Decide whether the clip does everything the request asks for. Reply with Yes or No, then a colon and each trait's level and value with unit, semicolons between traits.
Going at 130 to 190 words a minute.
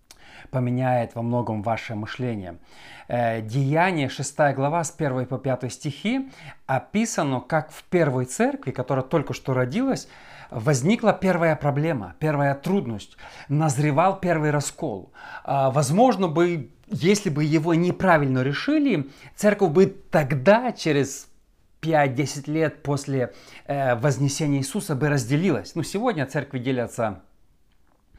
No: average, 115 wpm